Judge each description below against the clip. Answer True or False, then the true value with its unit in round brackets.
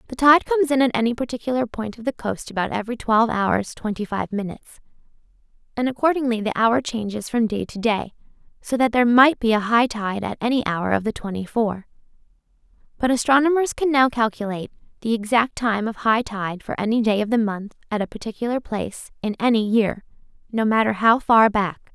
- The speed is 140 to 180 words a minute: False (195 wpm)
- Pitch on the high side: True (225 Hz)